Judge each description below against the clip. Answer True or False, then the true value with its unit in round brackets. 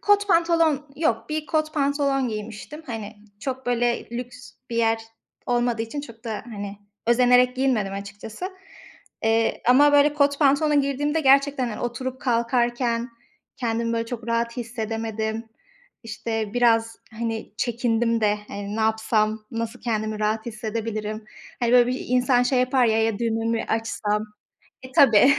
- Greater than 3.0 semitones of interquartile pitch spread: False (2.7 semitones)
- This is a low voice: False (235 Hz)